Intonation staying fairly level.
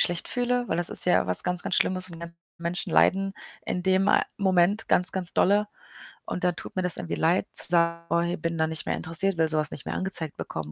Yes: narrow, 2.2 semitones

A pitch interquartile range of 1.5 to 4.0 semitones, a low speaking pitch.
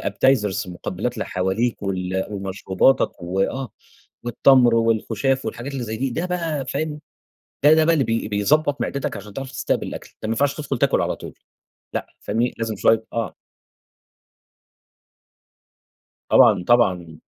No: average, 5.3 semitones; low, 115 Hz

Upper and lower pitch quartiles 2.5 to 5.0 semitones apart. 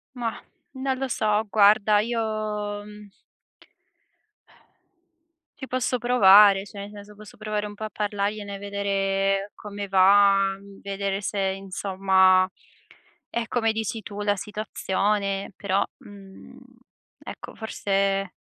No: narrow, 1.5 semitones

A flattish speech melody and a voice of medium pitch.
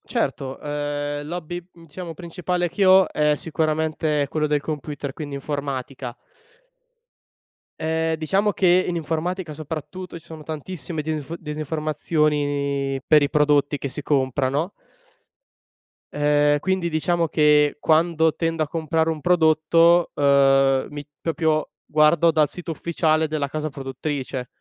Yes: narrow, 2.2 semitones; medium, 155 Hz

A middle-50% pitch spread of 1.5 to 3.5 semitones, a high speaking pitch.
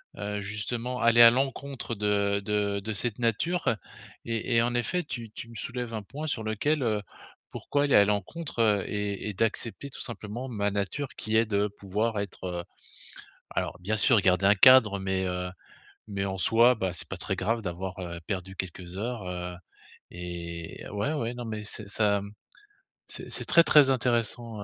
No: average, 3.2 semitones; low, 105 Hz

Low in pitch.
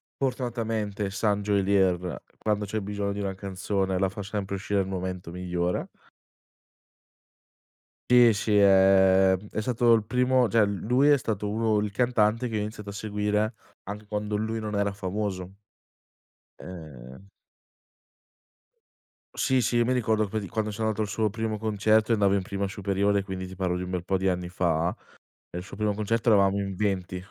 Yes: low, 100 Hz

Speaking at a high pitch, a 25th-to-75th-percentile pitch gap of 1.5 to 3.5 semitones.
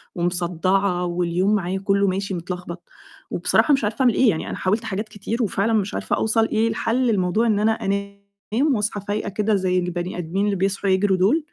Yes: high, 200 Hz; average, 2.9 semitones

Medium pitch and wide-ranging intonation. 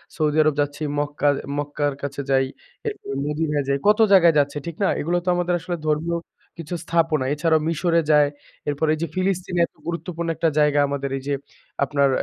No: medium, 155 Hz; average, 2.8 semitones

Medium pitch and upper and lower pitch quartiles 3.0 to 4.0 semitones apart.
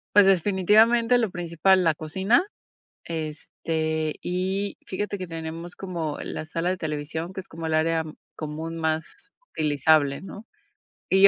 Yes: medium, 165 Hz; average, 3.3 semitones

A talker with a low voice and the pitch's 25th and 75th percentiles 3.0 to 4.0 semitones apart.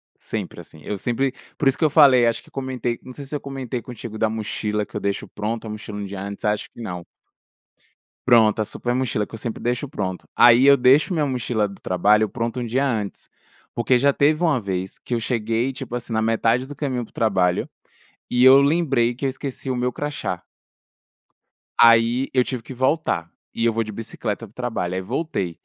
Yes: low, 120 Hz; average, 3.6 semitones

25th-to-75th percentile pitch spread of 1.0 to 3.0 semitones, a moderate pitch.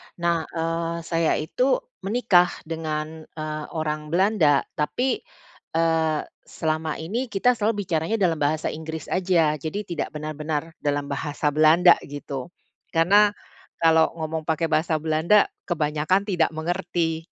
Yes: narrow, 2.4 semitones; medium, 160 Hz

